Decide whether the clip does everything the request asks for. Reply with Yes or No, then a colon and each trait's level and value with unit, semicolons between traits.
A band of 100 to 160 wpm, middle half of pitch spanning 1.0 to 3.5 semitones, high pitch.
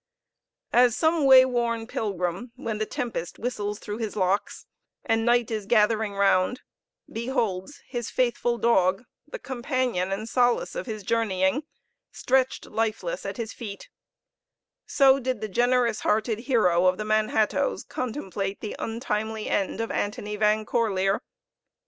Yes: slow, 135 wpm; average, 3.0 semitones; high, 225 Hz